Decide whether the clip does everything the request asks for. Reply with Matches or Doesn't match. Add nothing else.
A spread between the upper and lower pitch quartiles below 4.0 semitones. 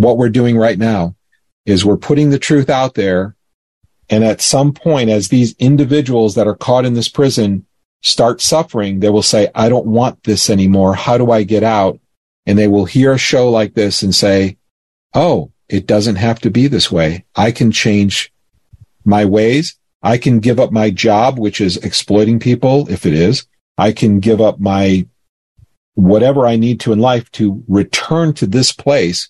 Matches